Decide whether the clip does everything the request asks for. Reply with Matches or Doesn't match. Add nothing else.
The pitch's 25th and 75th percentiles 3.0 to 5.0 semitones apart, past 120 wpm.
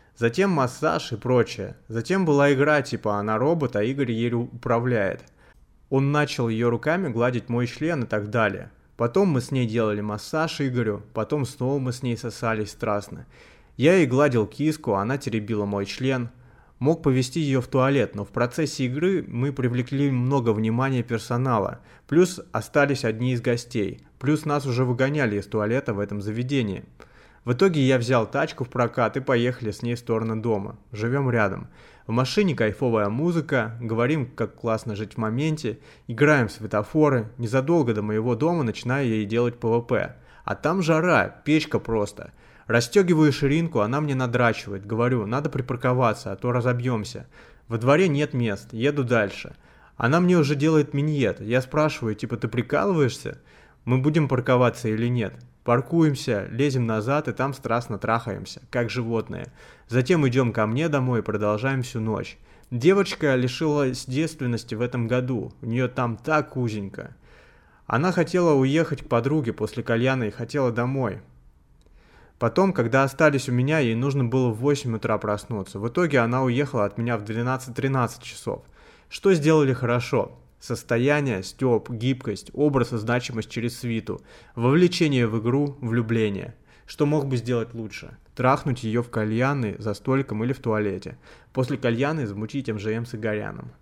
Matches